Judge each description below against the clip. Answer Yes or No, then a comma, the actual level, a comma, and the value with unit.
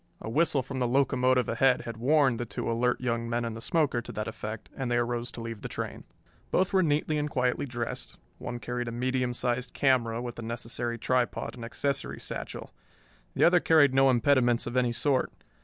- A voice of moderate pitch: No, low, 125 Hz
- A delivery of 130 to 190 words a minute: No, fast, 205 wpm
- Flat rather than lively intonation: Yes, narrow, 2.2 semitones